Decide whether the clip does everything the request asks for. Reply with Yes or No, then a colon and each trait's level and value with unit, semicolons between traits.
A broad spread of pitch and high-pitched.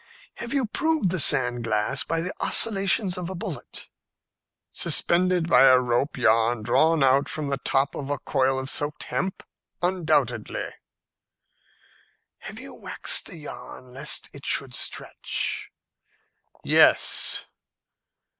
No: wide, 5.7 semitones; medium, 145 Hz